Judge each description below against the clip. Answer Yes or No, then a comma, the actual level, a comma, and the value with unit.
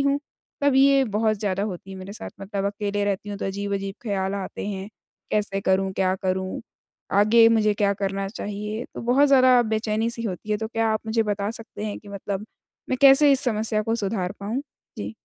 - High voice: Yes, high, 210 Hz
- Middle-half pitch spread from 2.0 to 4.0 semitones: Yes, narrow, 2.5 semitones